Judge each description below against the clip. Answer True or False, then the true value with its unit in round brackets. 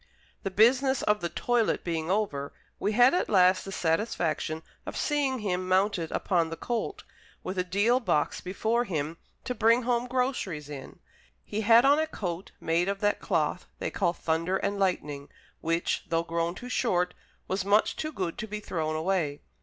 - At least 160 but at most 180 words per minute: True (175 wpm)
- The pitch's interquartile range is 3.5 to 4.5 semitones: False (5.6 semitones)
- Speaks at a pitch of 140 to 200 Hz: True (190 Hz)